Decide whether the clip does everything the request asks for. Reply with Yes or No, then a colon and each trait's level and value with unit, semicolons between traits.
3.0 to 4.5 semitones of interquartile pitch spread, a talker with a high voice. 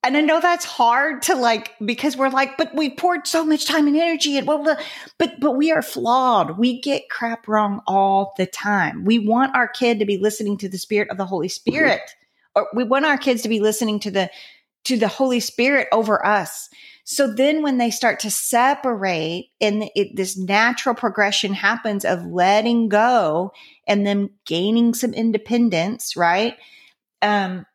No: average, 5.0 semitones; high, 235 Hz